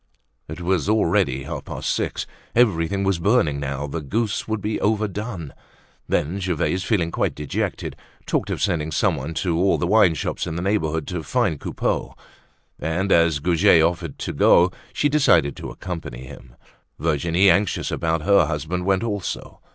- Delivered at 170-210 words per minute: No, average, 160 wpm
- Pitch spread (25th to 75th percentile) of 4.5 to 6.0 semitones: No, average, 4.0 semitones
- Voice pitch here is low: Yes, very low, 85 Hz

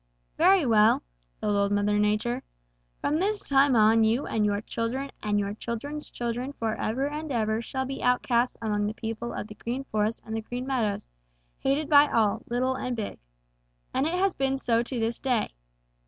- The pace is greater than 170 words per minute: Yes, average, 185 wpm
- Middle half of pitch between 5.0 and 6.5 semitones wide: No, average, 3.8 semitones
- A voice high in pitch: Yes, high, 235 Hz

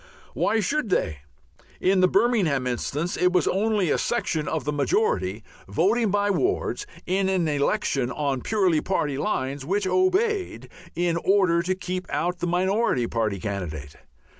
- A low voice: No, medium, 180 Hz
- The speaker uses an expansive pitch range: Yes, wide, 6.4 semitones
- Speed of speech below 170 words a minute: Yes, average, 150 wpm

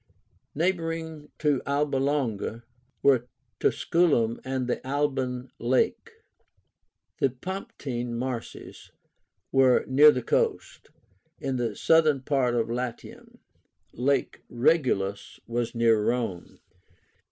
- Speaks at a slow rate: Yes, slow, 95 wpm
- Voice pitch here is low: Yes, low, 130 Hz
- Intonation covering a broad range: No, average, 3.4 semitones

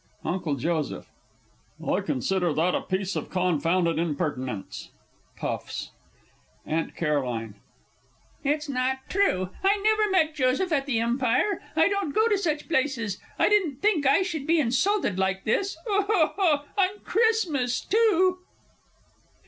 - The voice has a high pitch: Yes, very high, 275 Hz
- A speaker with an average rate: No, slow, 130 wpm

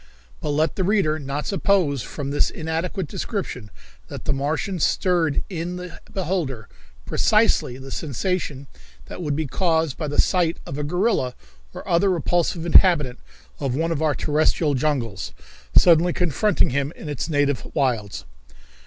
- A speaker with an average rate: Yes, average, 150 wpm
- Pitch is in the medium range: Yes, medium, 155 Hz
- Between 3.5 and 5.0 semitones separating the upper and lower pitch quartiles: Yes, average, 4.1 semitones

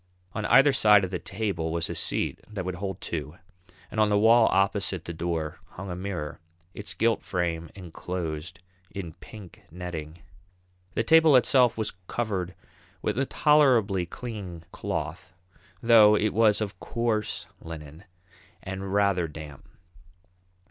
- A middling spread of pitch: Yes, average, 4.2 semitones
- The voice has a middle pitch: No, very low, 95 Hz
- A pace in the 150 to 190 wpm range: No, average, 140 wpm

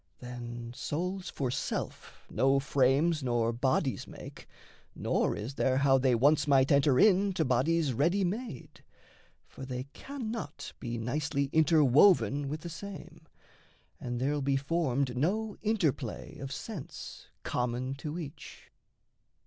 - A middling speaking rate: No, slow, 130 wpm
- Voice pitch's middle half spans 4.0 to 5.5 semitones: Yes, average, 4.6 semitones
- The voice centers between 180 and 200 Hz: No, medium, 140 Hz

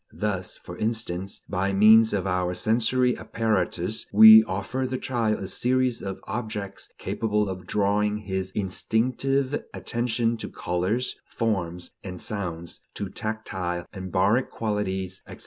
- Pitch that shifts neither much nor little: Yes, average, 3.3 semitones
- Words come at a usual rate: No, slow, 130 wpm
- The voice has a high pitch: No, low, 105 Hz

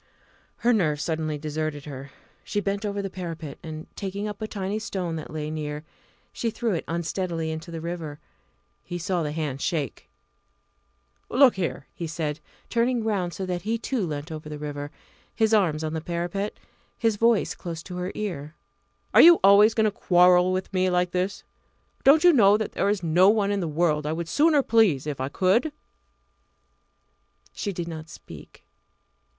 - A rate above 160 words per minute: Yes, average, 180 wpm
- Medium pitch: Yes, medium, 180 Hz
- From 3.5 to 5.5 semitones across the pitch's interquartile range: Yes, average, 4.7 semitones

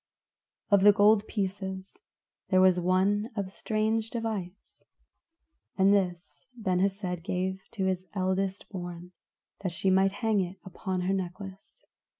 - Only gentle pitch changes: Yes, narrow, 1.6 semitones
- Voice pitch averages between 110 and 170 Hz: No, high, 190 Hz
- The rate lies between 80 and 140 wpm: Yes, slow, 135 wpm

